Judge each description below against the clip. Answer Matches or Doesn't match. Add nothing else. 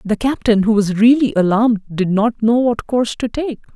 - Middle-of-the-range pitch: Doesn't match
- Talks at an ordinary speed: Doesn't match